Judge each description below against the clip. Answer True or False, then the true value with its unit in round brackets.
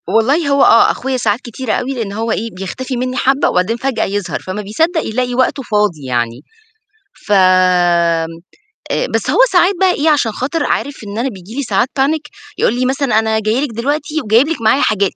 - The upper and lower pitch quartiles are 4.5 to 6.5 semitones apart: True (5.1 semitones)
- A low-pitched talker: False (230 Hz)